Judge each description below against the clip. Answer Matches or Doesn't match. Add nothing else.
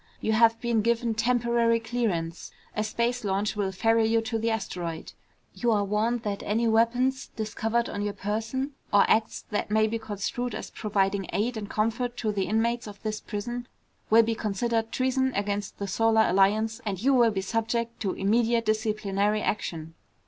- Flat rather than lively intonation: Matches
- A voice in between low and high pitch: Doesn't match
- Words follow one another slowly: Doesn't match